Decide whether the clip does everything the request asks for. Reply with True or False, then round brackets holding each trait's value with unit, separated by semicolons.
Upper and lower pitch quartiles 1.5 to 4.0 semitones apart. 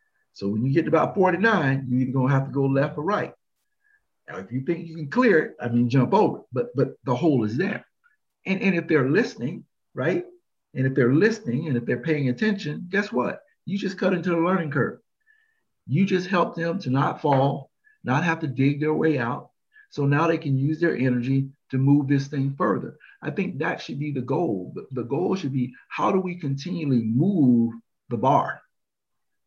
False (5.6 semitones)